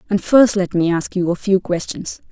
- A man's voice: No, female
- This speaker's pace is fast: Yes, fast, 235 wpm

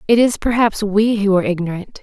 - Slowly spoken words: No, fast, 205 wpm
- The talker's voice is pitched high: Yes, high, 205 Hz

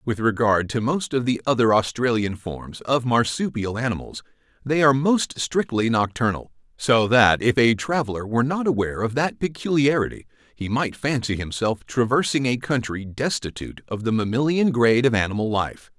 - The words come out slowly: No, average, 160 wpm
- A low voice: Yes, low, 120 Hz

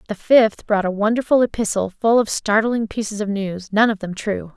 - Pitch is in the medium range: No, high, 210 Hz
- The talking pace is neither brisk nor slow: No, fast, 210 wpm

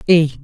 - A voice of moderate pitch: Yes, medium, 155 Hz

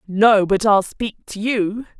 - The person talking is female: Yes, female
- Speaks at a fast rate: No, average, 180 wpm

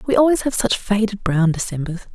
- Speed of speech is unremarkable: Yes, average, 195 wpm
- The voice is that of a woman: Yes, female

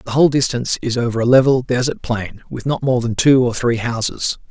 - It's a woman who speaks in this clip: No, male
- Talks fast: Yes, fast, 225 wpm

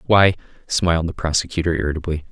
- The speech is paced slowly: Yes, slow, 130 wpm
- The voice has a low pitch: Yes, very low, 85 Hz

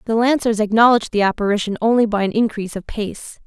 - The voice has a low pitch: No, high, 215 Hz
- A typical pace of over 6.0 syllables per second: Yes, 6.5 syllables/s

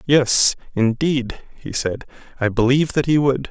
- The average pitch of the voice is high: No, low, 130 Hz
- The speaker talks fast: No, average, 155 wpm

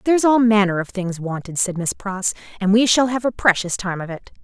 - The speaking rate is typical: No, fast, 245 wpm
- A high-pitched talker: Yes, high, 205 Hz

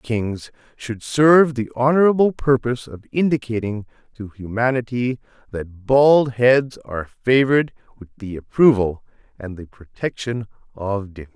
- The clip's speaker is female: No, male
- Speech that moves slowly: Yes, slow, 120 wpm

